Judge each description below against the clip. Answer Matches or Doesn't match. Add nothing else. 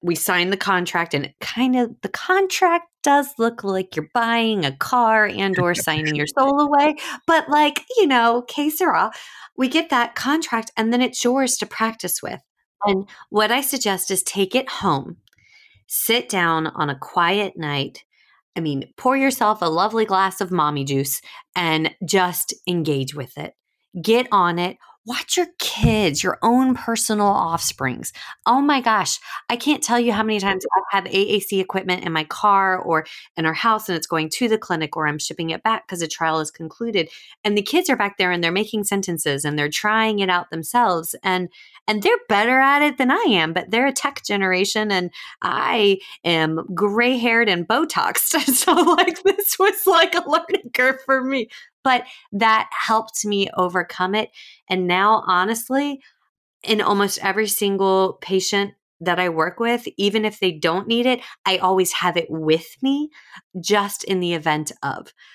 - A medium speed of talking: Matches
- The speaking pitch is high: Matches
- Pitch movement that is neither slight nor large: Doesn't match